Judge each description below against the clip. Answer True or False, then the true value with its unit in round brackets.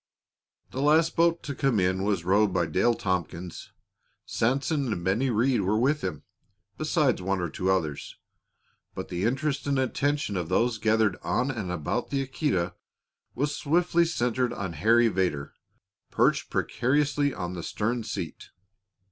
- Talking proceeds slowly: False (150 wpm)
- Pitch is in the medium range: False (115 Hz)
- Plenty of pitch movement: True (6.8 semitones)